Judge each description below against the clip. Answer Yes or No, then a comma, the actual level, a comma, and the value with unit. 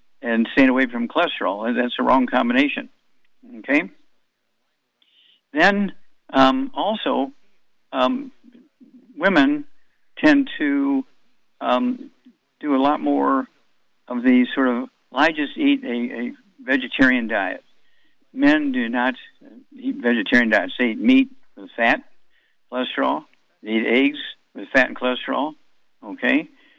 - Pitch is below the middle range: No, very high, 255 Hz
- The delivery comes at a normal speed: No, slow, 120 wpm